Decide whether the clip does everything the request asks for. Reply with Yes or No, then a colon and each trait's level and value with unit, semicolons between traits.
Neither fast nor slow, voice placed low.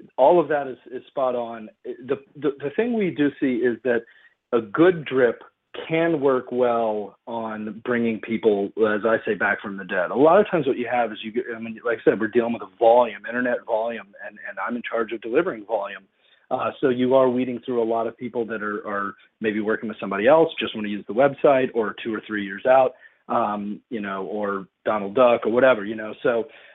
No: fast, 230 wpm; low, 115 Hz